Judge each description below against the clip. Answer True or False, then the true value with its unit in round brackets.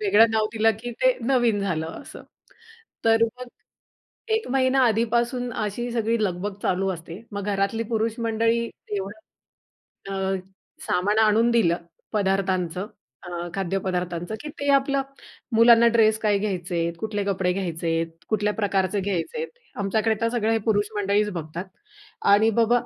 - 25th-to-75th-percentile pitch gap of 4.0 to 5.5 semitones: False (3.1 semitones)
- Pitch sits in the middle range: False (210 Hz)